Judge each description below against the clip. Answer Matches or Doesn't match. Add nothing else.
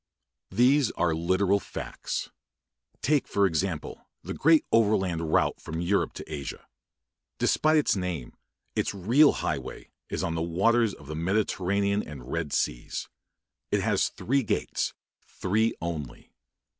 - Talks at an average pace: Doesn't match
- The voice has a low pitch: Matches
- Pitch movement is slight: Doesn't match